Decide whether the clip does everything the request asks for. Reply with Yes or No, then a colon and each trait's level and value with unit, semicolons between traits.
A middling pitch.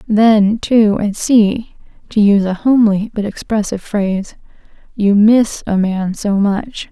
No: high, 210 Hz